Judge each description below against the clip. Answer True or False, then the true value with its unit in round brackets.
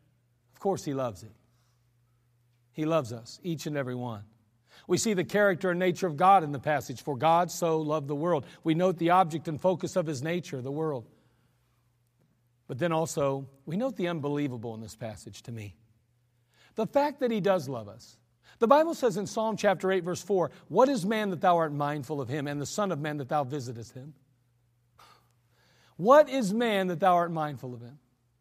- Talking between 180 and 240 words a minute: True (200 wpm)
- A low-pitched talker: False (145 Hz)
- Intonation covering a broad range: True (6.8 semitones)